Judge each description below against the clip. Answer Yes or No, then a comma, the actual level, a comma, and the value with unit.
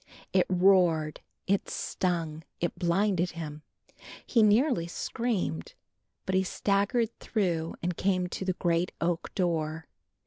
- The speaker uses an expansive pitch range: No, average, 2.9 semitones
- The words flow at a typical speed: No, slow, 125 wpm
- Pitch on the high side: No, medium, 180 Hz